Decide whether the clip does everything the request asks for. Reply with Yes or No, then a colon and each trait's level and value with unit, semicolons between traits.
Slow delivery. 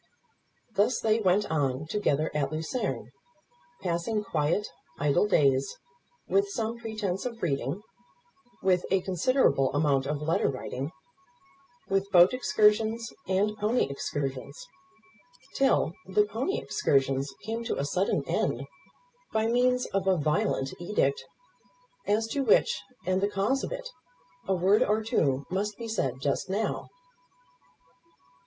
Yes: slow, 130 wpm